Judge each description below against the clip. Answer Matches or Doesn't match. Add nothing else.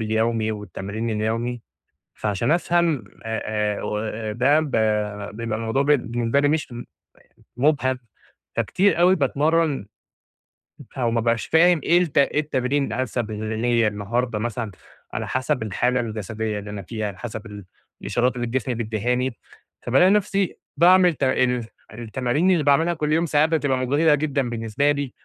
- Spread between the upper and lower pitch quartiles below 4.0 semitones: Doesn't match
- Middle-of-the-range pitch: Doesn't match